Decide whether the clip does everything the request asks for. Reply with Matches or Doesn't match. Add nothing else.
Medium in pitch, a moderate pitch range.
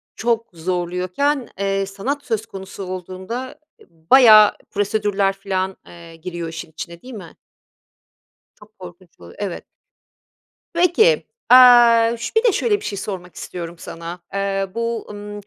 Doesn't match